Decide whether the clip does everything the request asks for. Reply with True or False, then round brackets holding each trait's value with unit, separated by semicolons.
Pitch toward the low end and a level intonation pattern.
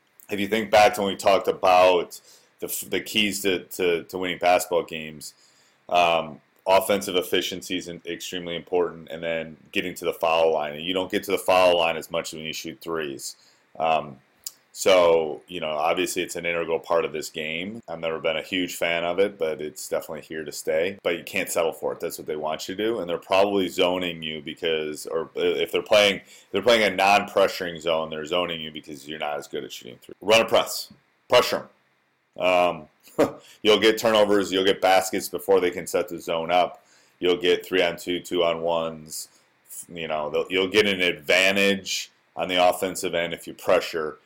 False (90 Hz; 3.5 semitones)